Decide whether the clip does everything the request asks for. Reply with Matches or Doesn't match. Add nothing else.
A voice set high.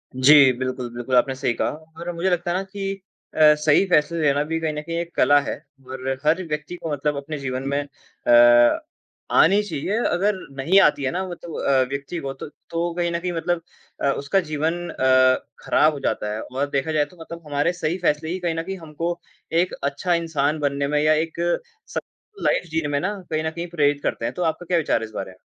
Doesn't match